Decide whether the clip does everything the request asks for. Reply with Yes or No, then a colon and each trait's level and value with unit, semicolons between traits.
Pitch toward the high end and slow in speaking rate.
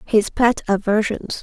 Yes: high, 215 Hz; slow, 125 wpm